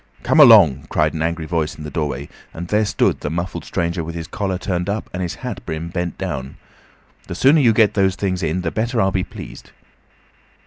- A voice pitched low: Yes, very low, 90 Hz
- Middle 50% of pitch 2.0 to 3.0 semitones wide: No, average, 3.8 semitones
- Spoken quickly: Yes, fast, 215 wpm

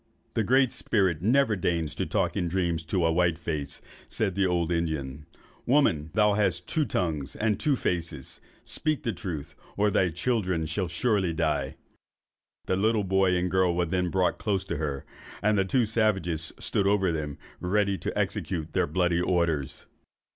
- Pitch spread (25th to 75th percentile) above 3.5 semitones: Yes, average, 4.0 semitones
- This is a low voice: Yes, very low, 90 Hz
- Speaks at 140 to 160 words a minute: No, average, 170 wpm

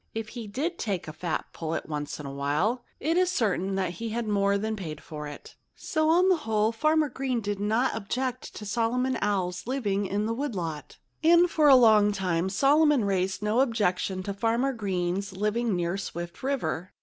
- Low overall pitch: No, high, 210 Hz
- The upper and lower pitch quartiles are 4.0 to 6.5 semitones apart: Yes, wide, 5.4 semitones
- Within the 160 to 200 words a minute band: Yes, average, 165 wpm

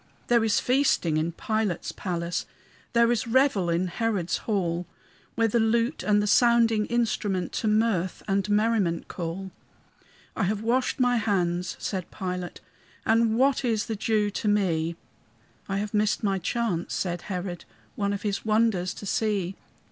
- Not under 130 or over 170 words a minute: Yes, average, 155 wpm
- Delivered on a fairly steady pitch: No, average, 3.8 semitones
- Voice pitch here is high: Yes, high, 205 Hz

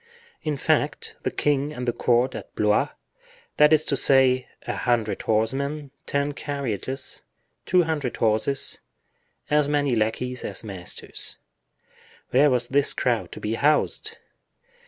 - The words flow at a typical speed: No, slow, 130 wpm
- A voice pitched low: Yes, low, 130 Hz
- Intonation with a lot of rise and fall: No, average, 3.5 semitones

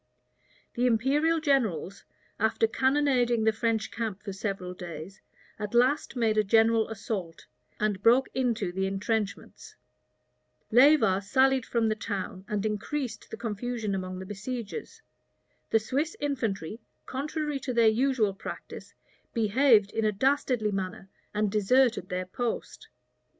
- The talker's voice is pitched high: Yes, high, 220 Hz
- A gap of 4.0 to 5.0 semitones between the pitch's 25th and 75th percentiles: Yes, average, 4.3 semitones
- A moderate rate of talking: No, slow, 130 wpm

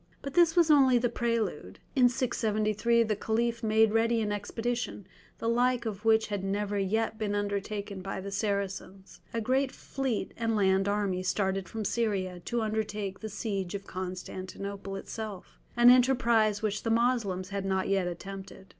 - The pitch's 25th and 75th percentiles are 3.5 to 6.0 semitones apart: No, average, 3.0 semitones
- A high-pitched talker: Yes, high, 210 Hz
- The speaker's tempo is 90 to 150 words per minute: No, average, 165 wpm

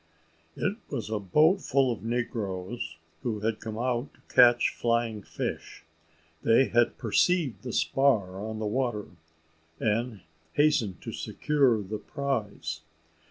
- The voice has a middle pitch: No, low, 115 Hz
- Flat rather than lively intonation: No, average, 3.5 semitones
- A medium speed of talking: No, slow, 130 wpm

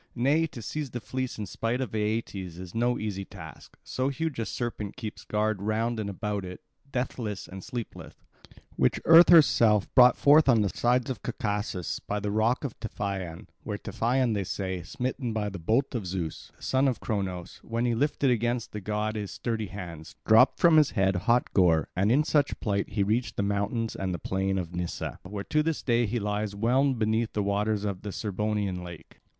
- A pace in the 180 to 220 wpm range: Yes, average, 195 wpm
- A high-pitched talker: No, low, 110 Hz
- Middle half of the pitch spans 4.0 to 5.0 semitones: No, average, 3.6 semitones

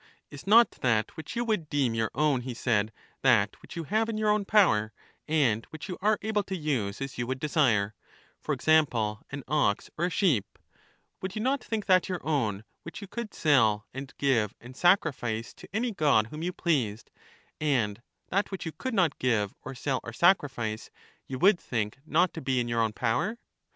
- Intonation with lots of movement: Yes, wide, 8.1 semitones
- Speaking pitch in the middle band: Yes, medium, 145 Hz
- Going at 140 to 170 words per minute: No, average, 200 wpm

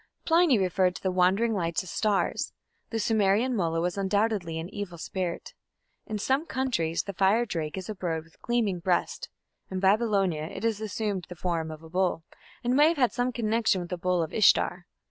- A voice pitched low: No, high, 190 Hz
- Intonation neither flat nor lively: Yes, average, 4.2 semitones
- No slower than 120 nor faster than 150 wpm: No, average, 190 wpm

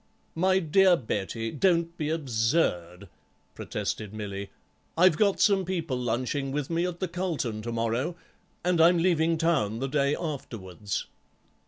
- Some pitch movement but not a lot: No, wide, 7.1 semitones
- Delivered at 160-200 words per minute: No, average, 140 wpm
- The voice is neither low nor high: Yes, medium, 150 Hz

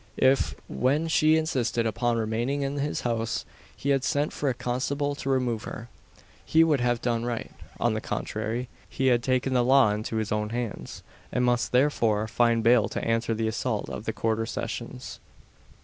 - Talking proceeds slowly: No, average, 180 wpm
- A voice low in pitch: Yes, low, 120 Hz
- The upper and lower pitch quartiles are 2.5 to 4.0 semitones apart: Yes, average, 3.1 semitones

